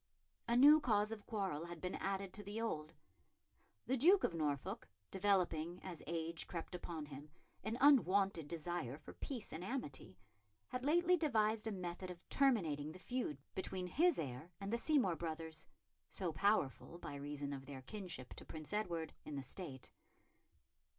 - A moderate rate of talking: Yes, average, 165 wpm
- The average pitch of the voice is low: No, medium, 180 Hz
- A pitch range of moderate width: No, wide, 5.8 semitones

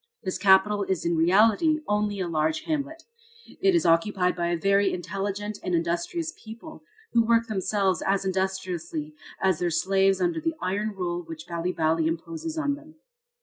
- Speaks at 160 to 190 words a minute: Yes, average, 165 wpm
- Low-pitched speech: No, high, 190 Hz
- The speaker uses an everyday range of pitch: Yes, average, 4.0 semitones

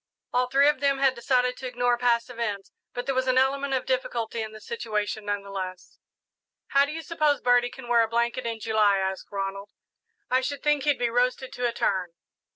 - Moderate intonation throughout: Yes, average, 3.4 semitones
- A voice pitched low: No, high, 245 Hz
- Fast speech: Yes, fast, 215 wpm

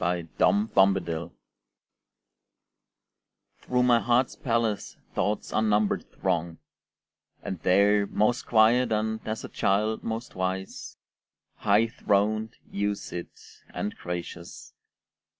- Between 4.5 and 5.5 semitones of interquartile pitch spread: No, average, 3.0 semitones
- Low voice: Yes, low, 105 Hz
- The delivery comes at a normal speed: No, slow, 100 wpm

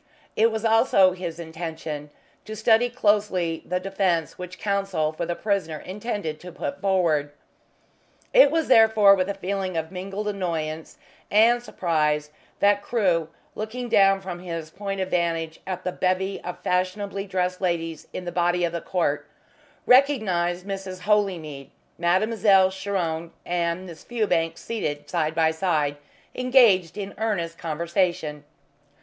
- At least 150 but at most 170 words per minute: No, average, 140 wpm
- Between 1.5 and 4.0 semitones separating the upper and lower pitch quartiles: Yes, average, 3.4 semitones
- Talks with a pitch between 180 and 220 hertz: Yes, medium, 185 Hz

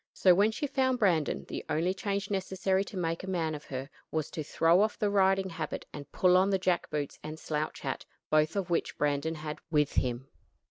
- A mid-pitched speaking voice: Yes, medium, 175 Hz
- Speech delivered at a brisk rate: Yes, fast, 215 wpm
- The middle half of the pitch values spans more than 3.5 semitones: Yes, average, 4.0 semitones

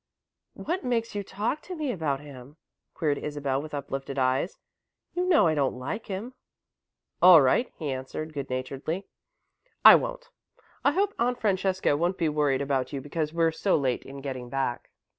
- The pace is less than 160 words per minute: No, average, 170 wpm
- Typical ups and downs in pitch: No, wide, 7.0 semitones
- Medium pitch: Yes, medium, 155 Hz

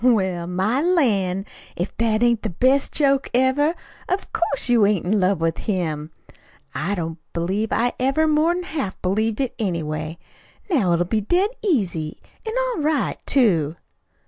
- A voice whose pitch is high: Yes, high, 215 Hz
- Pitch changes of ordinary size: No, wide, 7.8 semitones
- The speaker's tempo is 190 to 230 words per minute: No, average, 160 wpm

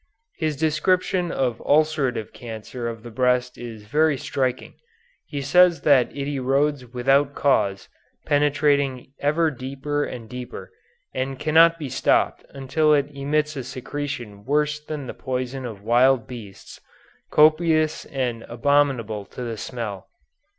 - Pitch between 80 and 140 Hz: Yes, low, 135 Hz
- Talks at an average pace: No, slow, 130 wpm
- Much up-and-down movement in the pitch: No, average, 3.4 semitones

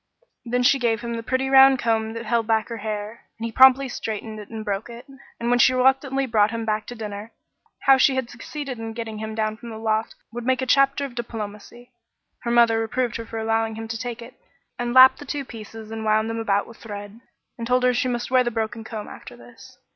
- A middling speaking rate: No, fast, 240 wpm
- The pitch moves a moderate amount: No, narrow, 2.3 semitones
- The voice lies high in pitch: Yes, high, 230 Hz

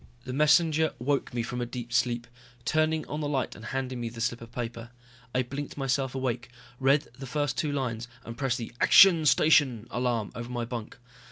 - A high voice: No, low, 125 Hz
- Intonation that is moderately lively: Yes, average, 3.3 semitones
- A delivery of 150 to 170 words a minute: No, average, 195 wpm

